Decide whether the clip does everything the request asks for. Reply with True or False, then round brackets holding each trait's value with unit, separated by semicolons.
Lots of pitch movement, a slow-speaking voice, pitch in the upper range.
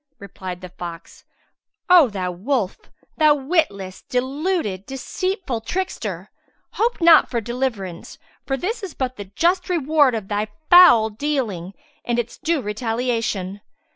True (7.7 semitones; 130 wpm; 245 Hz)